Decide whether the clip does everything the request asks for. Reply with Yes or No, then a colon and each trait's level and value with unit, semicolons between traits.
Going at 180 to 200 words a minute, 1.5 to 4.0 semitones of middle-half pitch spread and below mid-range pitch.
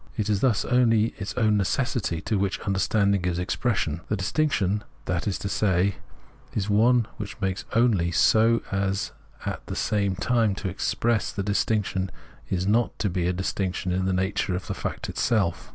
Yes: average, 185 wpm; average, 2.8 semitones; low, 100 Hz